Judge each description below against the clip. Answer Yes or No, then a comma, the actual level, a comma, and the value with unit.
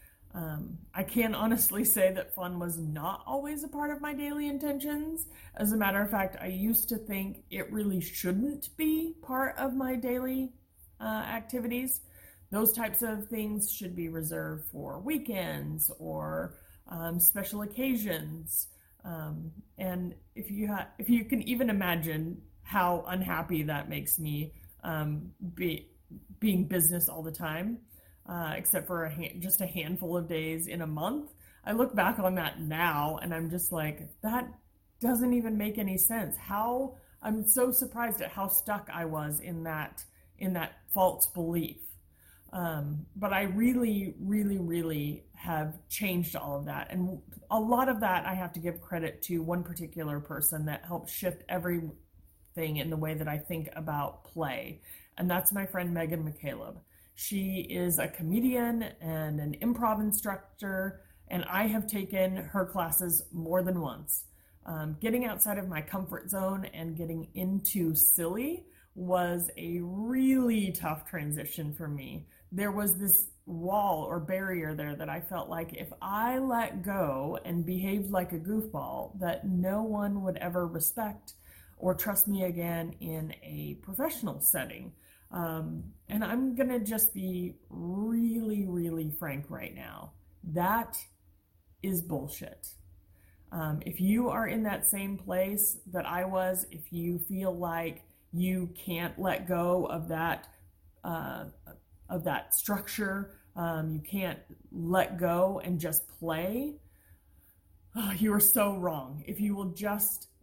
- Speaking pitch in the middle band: Yes, medium, 180 Hz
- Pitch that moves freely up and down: No, average, 4.5 semitones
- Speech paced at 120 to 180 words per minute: Yes, average, 155 wpm